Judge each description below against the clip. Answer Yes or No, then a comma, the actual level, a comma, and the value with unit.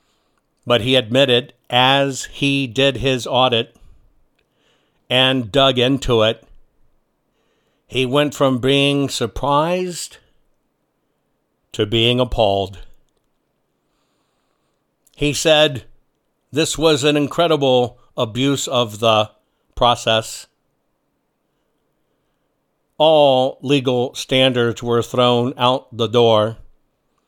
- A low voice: Yes, low, 130 Hz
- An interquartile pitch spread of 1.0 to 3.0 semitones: Yes, narrow, 2.6 semitones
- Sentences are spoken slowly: Yes, slow, 85 wpm